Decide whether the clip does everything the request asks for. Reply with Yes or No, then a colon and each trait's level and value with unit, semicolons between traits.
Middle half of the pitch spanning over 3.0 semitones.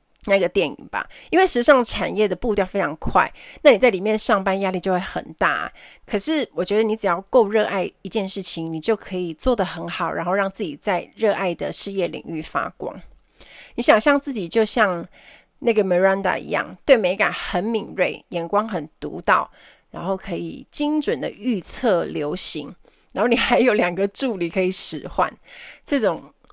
Yes: average, 3.7 semitones